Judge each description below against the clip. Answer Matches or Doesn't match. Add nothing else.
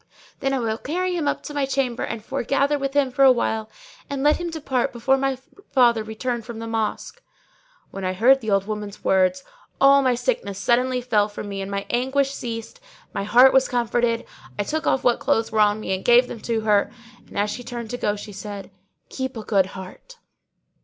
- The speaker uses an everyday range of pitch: Matches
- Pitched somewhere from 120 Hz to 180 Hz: Doesn't match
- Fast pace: Matches